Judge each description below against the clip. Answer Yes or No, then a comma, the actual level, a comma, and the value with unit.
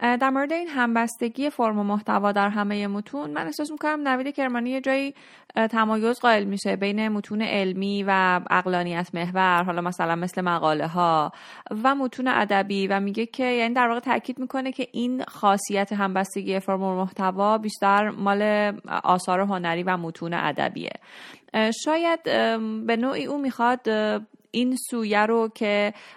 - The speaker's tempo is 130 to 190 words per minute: Yes, average, 150 wpm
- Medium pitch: No, high, 215 Hz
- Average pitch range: Yes, average, 4.2 semitones